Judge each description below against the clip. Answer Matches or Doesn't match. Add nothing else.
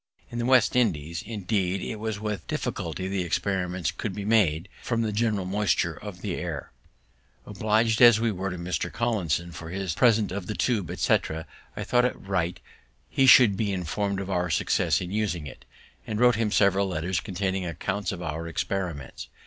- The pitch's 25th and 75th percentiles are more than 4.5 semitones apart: Doesn't match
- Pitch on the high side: Doesn't match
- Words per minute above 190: Doesn't match